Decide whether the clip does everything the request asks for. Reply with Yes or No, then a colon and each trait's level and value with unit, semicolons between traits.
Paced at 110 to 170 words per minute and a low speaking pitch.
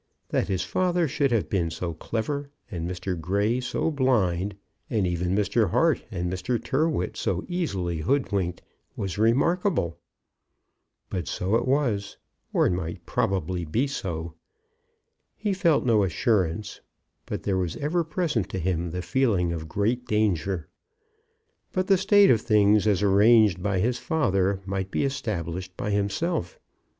Yes: average, 145 wpm; low, 100 Hz